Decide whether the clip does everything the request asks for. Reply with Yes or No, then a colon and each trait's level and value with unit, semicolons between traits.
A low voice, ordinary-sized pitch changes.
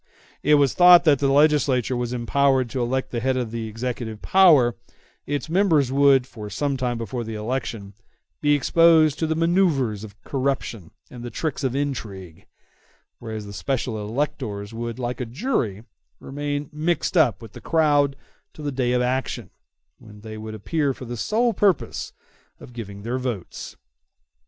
Yes: low, 130 Hz; average, 4.4 semitones